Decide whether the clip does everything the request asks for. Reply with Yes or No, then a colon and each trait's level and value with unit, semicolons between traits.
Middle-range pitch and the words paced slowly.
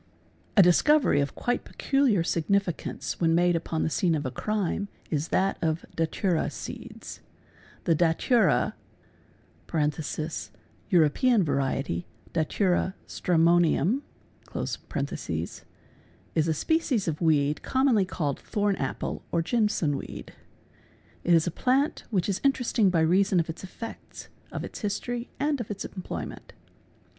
Yes: medium, 175 Hz; slow, 125 wpm